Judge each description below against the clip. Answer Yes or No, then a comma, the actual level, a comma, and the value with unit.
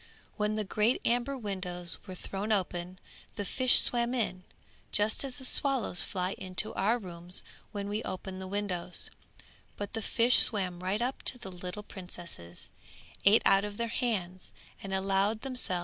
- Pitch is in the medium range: No, high, 200 Hz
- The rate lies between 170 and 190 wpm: Yes, average, 175 wpm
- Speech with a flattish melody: No, average, 3.7 semitones